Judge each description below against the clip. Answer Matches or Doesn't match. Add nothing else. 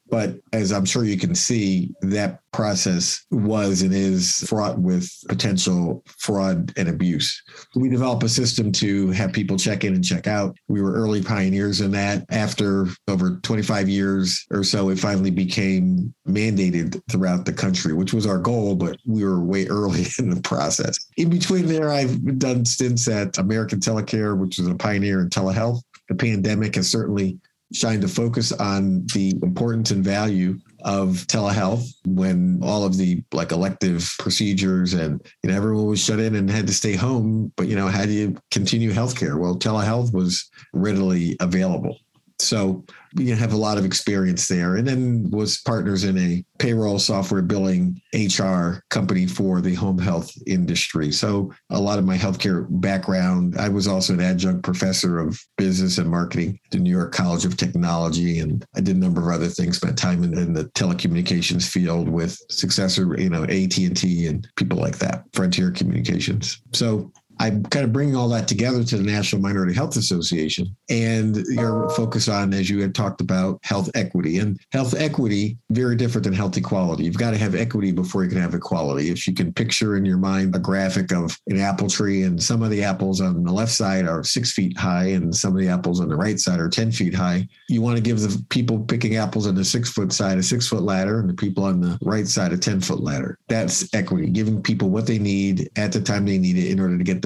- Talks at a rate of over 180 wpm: Matches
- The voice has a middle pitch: Doesn't match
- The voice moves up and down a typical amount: Matches